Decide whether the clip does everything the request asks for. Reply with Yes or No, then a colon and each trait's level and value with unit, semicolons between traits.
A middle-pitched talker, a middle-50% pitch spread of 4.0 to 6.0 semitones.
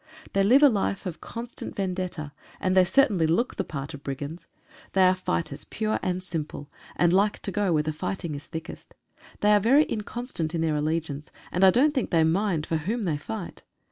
Yes: medium, 180 Hz; average, 4.8 semitones